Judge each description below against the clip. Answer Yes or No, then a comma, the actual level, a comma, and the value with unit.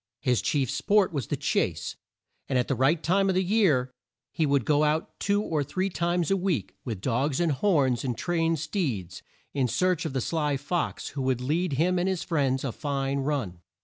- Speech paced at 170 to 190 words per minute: No, fast, 205 wpm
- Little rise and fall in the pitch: No, average, 4.9 semitones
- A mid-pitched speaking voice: Yes, medium, 150 Hz